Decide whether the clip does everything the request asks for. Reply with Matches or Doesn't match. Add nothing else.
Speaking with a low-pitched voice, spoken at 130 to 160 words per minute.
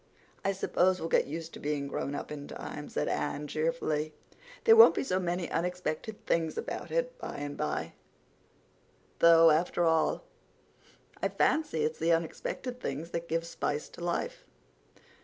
Doesn't match